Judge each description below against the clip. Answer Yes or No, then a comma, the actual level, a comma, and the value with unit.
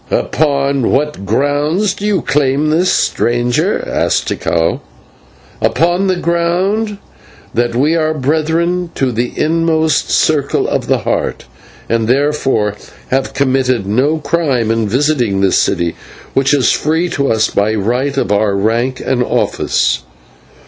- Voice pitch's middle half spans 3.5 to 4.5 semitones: No, average, 5.1 semitones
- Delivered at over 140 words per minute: No, slow, 135 wpm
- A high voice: No, medium, 140 Hz